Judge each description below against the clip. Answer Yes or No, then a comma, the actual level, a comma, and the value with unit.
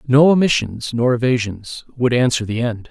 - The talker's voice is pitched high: No, low, 125 Hz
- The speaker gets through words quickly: No, average, 165 wpm